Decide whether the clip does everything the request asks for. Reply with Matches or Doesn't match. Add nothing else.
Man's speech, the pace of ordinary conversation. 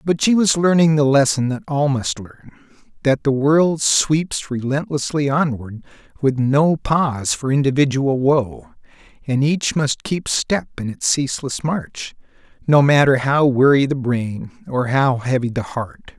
Matches